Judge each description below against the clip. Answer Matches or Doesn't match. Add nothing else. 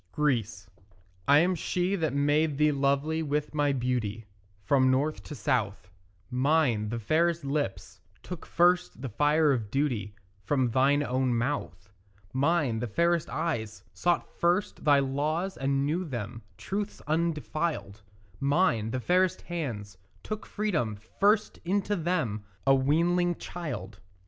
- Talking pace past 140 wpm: Doesn't match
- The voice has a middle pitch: Matches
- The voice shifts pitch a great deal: Matches